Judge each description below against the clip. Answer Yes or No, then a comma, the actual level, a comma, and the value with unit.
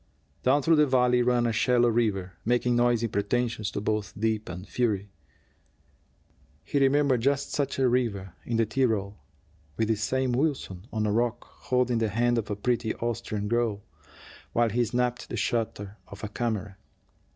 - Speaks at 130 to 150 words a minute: No, average, 165 wpm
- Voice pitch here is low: Yes, low, 115 Hz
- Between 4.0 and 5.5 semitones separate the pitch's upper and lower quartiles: No, average, 2.7 semitones